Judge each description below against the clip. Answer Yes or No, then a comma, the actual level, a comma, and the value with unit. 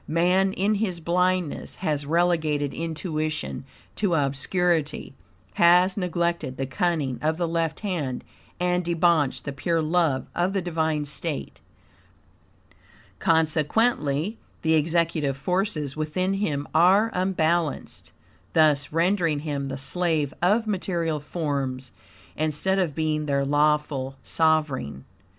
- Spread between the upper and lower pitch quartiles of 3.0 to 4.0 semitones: Yes, average, 3.3 semitones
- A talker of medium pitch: Yes, medium, 160 Hz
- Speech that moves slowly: Yes, slow, 115 wpm